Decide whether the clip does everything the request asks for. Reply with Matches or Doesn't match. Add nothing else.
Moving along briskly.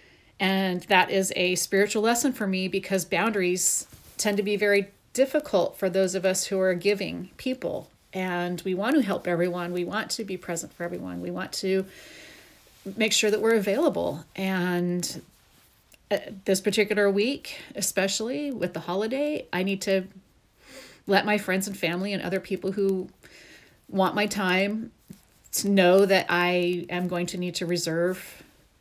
Doesn't match